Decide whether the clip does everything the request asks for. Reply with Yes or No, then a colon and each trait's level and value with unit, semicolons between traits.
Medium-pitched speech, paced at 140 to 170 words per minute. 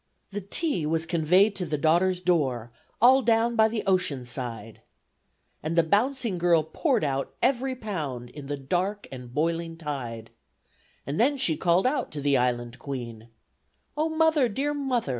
Yes: medium, 170 Hz; average, 160 wpm